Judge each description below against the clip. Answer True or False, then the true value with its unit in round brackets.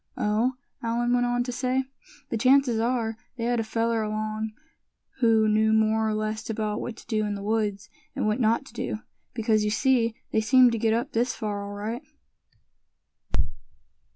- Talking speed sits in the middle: True (180 wpm)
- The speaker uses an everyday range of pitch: False (1.9 semitones)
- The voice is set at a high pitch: True (225 Hz)